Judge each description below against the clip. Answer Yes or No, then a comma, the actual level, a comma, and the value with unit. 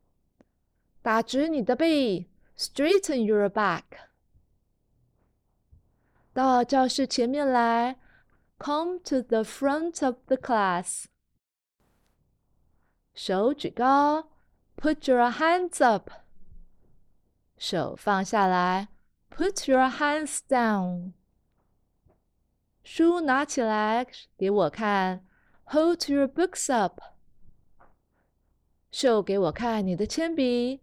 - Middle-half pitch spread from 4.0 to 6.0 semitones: Yes, wide, 5.6 semitones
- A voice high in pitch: Yes, very high, 255 Hz